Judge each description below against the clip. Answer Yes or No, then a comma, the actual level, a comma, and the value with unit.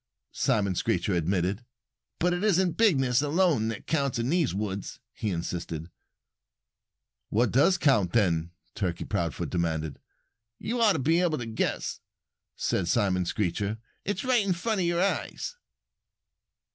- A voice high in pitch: No, low, 115 Hz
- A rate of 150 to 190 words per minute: No, average, 140 wpm